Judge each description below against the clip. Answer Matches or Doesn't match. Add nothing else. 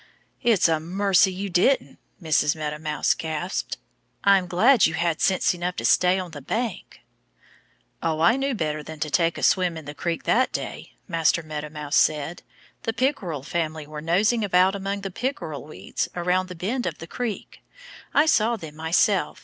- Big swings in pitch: Doesn't match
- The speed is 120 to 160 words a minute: Doesn't match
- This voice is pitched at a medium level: Matches